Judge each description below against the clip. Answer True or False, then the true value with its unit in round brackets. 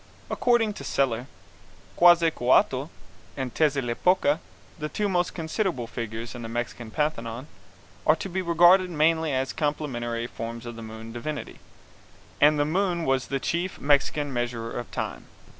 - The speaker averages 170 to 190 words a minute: False (140 wpm)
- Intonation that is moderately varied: False (5.8 semitones)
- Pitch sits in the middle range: True (145 Hz)